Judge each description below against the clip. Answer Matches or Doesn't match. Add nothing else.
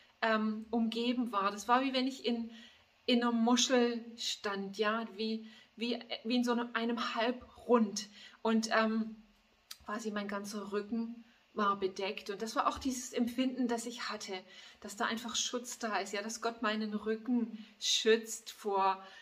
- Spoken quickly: Doesn't match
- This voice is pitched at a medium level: Doesn't match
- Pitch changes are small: Matches